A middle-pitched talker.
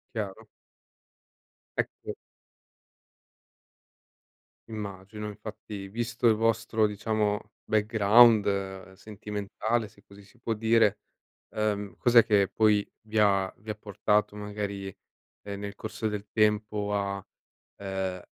No: low, 105 Hz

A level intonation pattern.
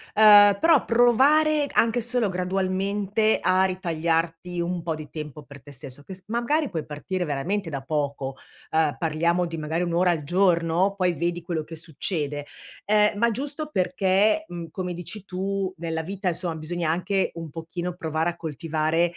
No: average, 3.7 semitones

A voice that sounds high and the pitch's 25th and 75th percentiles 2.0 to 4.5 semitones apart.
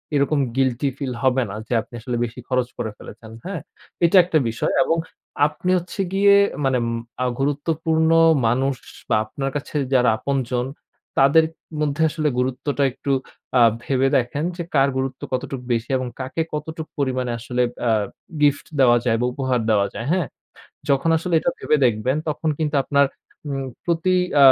No: low, 135 Hz; average, 3.4 semitones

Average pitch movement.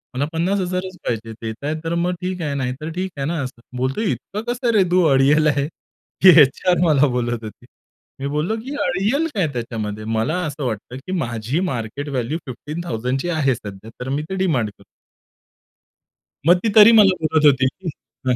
No: wide, 6.3 semitones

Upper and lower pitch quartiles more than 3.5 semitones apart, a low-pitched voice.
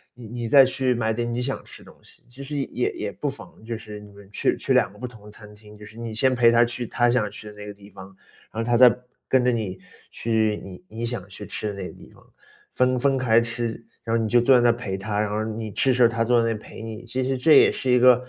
No: average, 2.7 semitones; low, 115 Hz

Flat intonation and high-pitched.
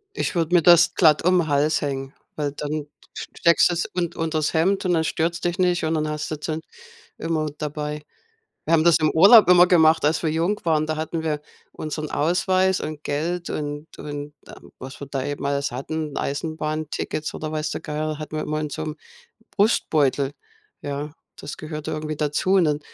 No: narrow, 2.0 semitones; medium, 155 Hz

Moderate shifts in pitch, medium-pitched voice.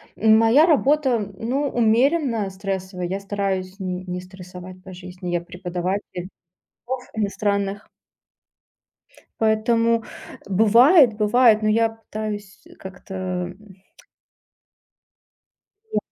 No: average, 3.5 semitones; high, 205 Hz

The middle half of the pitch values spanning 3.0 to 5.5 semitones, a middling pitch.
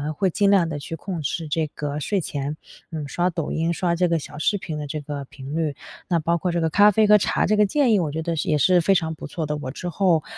Yes: average, 3.5 semitones; medium, 165 Hz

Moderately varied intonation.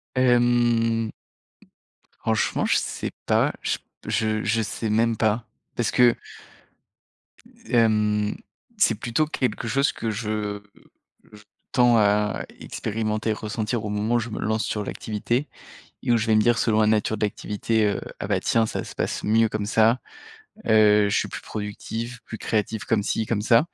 No: narrow, 1.7 semitones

